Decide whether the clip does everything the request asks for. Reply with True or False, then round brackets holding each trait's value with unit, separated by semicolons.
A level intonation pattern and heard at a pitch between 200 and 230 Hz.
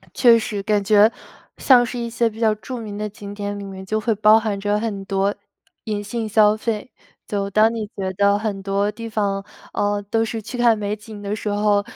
True (1.7 semitones; 210 Hz)